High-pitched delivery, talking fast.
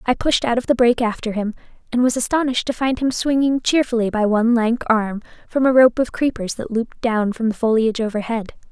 Yes: high, 235 Hz; fast, 220 wpm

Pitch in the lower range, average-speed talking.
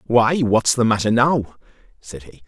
Yes: low, 115 Hz; average, 170 wpm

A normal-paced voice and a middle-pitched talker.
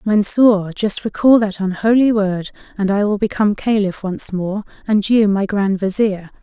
No: average, 170 wpm; high, 205 Hz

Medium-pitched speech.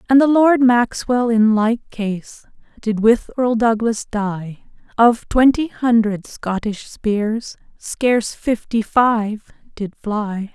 No: high, 225 Hz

